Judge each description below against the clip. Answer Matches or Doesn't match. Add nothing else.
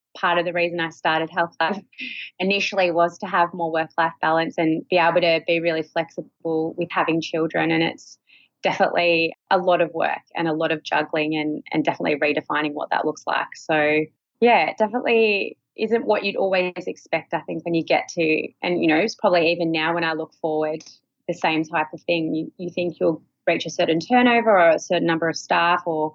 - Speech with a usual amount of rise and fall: Doesn't match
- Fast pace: Matches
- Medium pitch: Matches